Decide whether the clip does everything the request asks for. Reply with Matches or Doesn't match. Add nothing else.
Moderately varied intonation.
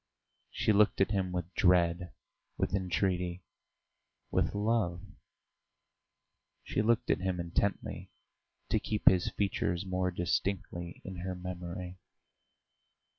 Doesn't match